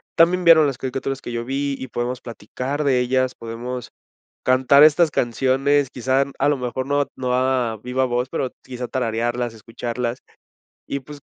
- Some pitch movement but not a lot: No, narrow, 2.3 semitones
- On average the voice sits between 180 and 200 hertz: No, low, 130 Hz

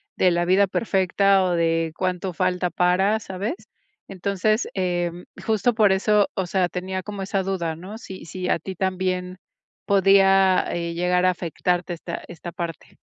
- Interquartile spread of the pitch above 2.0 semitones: No, narrow, 1.6 semitones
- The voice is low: No, medium, 185 Hz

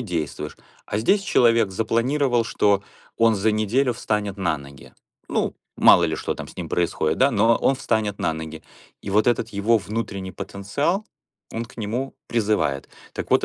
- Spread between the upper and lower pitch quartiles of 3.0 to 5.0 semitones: Yes, average, 3.4 semitones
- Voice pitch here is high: No, low, 110 Hz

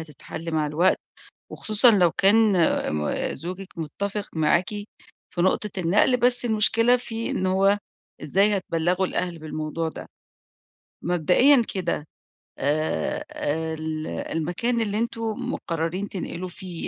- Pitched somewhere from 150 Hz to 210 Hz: Yes, medium, 185 Hz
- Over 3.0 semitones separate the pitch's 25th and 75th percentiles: Yes, average, 4.4 semitones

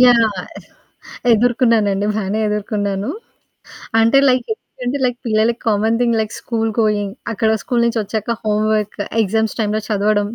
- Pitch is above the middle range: Yes, high, 220 Hz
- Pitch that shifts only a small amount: Yes, narrow, 1.8 semitones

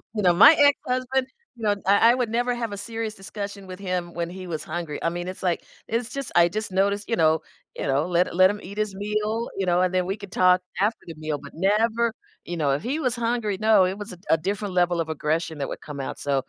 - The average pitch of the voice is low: No, high, 195 Hz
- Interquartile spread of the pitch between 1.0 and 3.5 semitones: No, average, 4.1 semitones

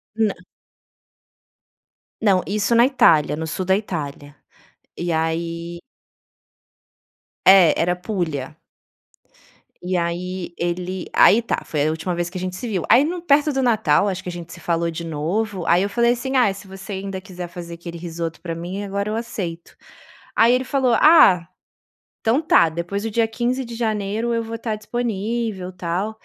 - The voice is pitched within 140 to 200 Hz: Yes, high, 190 Hz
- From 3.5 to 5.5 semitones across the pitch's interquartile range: Yes, average, 4.7 semitones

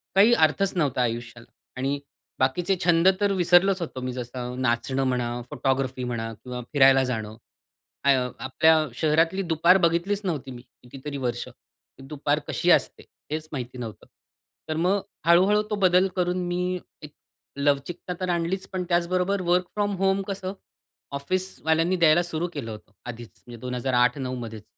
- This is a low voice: No, medium, 155 Hz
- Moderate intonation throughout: No, wide, 6.1 semitones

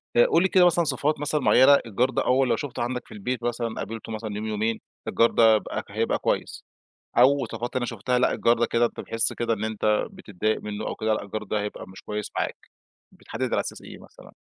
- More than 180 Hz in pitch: No, low, 115 Hz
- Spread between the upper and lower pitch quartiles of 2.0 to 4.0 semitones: Yes, average, 2.7 semitones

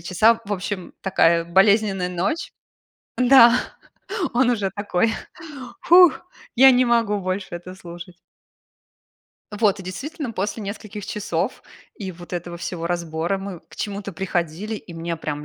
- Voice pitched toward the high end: Yes, high, 195 Hz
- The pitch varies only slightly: No, average, 3.9 semitones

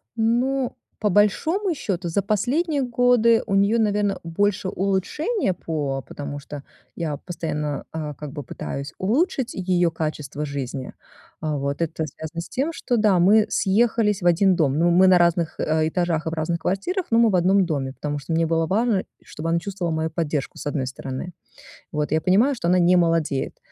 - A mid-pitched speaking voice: Yes, medium, 175 Hz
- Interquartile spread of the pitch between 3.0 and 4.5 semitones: No, average, 5.2 semitones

